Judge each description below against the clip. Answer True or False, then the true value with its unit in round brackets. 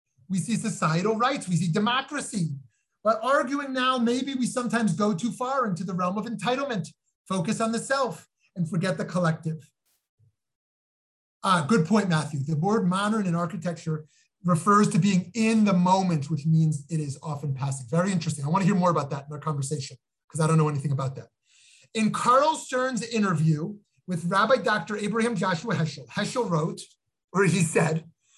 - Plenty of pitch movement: True (5.8 semitones)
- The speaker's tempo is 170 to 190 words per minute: True (180 wpm)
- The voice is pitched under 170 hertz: False (185 Hz)